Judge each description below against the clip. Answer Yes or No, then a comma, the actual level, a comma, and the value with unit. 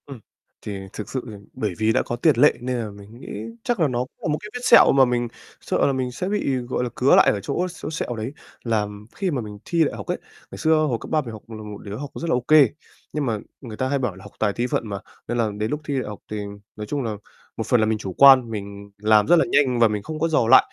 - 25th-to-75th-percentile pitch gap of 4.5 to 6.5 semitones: Yes, average, 4.8 semitones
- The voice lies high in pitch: No, low, 120 Hz